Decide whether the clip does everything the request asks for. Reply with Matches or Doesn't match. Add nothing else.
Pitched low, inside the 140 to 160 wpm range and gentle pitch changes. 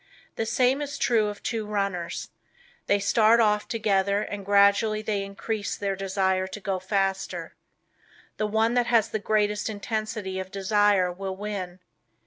Doesn't match